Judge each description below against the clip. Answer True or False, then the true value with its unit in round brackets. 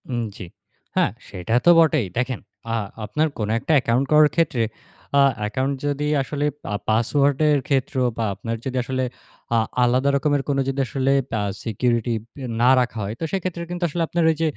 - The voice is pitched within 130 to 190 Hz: True (135 Hz)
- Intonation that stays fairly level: False (3.8 semitones)